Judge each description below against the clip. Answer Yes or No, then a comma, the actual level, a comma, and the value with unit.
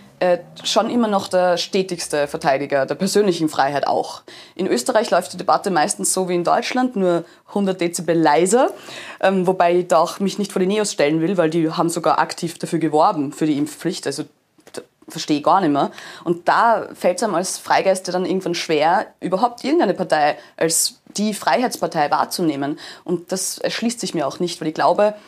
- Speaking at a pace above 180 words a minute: Yes, fast, 190 wpm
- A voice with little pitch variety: No, average, 3.2 semitones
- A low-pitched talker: No, medium, 180 Hz